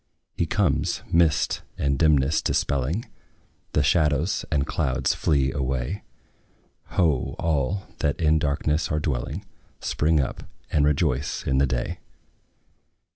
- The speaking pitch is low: Yes, very low, 75 Hz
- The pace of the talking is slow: Yes, slow, 120 wpm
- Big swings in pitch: No, average, 2.7 semitones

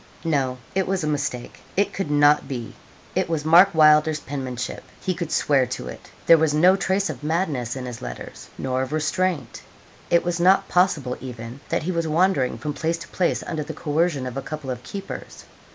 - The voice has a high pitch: No, medium, 150 Hz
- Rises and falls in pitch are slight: No, average, 4.6 semitones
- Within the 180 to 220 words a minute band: Yes, average, 200 wpm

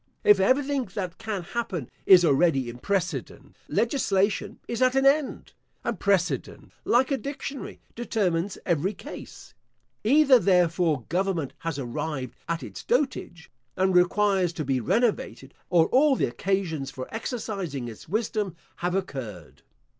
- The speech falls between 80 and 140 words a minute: Yes, slow, 135 wpm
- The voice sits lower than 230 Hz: Yes, high, 190 Hz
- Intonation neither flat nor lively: No, wide, 6.1 semitones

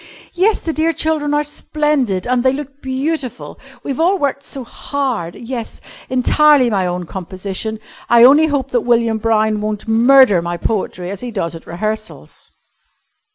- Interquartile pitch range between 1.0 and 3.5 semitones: No, average, 5.0 semitones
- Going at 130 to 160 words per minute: Yes, average, 155 wpm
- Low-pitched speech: No, high, 245 Hz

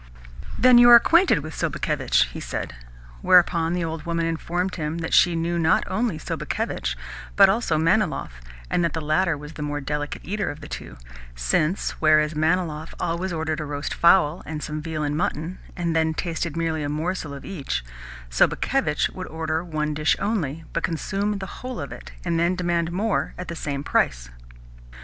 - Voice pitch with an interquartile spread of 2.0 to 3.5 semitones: Yes, average, 2.8 semitones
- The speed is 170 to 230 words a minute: Yes, average, 180 wpm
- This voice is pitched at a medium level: Yes, medium, 165 Hz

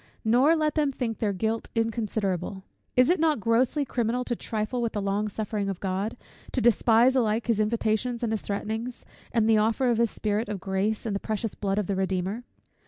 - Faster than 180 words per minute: Yes, average, 200 wpm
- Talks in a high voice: Yes, high, 220 Hz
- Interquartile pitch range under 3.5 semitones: Yes, average, 2.7 semitones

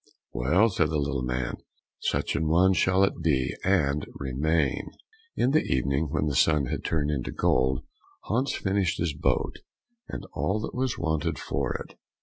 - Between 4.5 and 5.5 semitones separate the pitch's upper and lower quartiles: Yes, average, 5.2 semitones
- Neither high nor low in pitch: No, very low, 75 Hz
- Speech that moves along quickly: No, average, 165 wpm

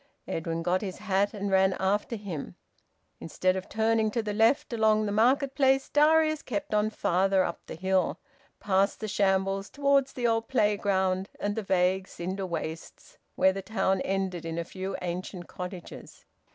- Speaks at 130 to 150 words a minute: No, average, 165 wpm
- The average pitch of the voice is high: Yes, high, 195 Hz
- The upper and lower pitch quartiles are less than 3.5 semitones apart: Yes, average, 2.8 semitones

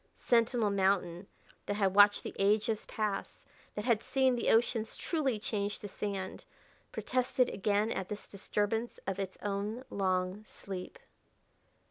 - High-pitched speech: Yes, high, 205 Hz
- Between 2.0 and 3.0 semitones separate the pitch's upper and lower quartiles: Yes, narrow, 2.4 semitones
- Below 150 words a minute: Yes, slow, 135 wpm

